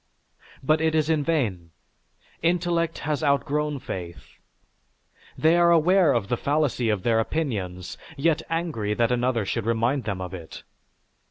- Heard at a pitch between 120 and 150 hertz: Yes, medium, 140 Hz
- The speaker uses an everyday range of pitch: No, wide, 6.2 semitones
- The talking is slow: No, average, 145 wpm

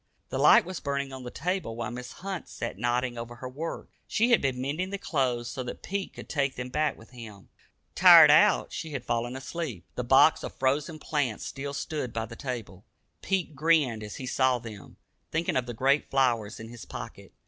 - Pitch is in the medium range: No, low, 130 Hz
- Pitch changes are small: No, average, 4.2 semitones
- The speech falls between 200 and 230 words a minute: Yes, fast, 205 wpm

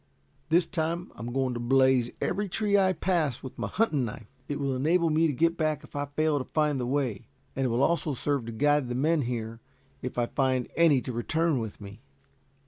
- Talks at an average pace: No, fast, 220 wpm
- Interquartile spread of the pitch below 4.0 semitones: No, average, 4.5 semitones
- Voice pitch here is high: No, medium, 140 Hz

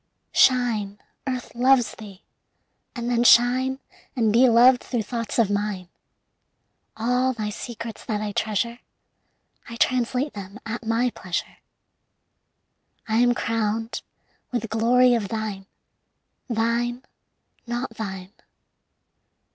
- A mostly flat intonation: Yes, narrow, 2.3 semitones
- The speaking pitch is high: Yes, high, 230 Hz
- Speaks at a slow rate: Yes, slow, 110 wpm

